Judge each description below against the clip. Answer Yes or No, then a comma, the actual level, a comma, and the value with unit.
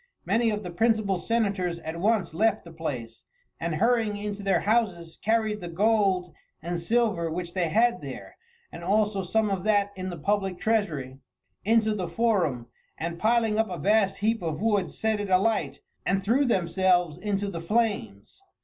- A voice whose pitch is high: Yes, high, 195 Hz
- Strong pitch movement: No, average, 4.2 semitones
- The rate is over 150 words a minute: Yes, average, 170 wpm